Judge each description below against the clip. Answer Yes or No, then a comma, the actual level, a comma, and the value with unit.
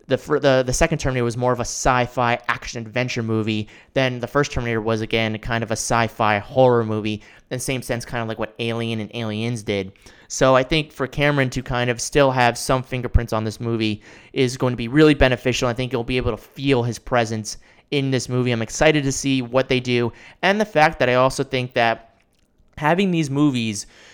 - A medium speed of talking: No, fast, 225 wpm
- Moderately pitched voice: No, low, 125 Hz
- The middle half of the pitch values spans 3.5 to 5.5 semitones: No, narrow, 2.5 semitones